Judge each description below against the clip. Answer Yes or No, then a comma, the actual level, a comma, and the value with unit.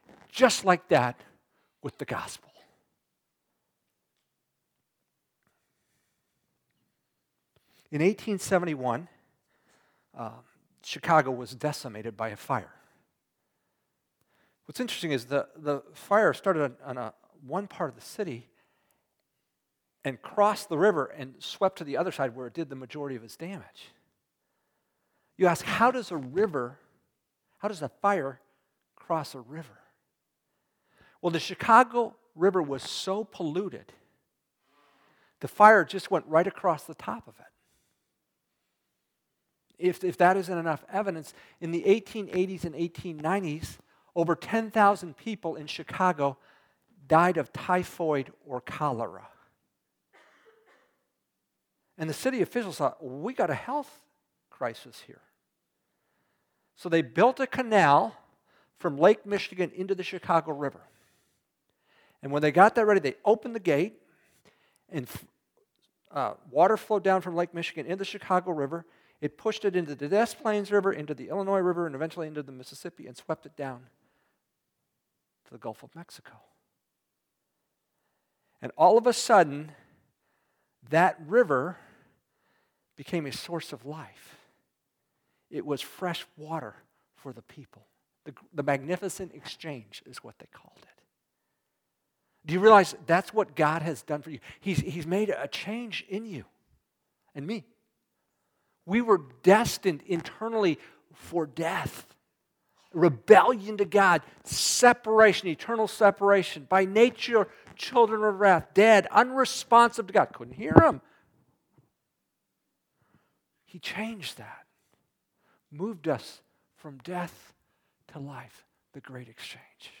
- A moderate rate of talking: No, slow, 125 wpm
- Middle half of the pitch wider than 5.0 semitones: Yes, wide, 5.5 semitones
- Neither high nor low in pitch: Yes, medium, 175 Hz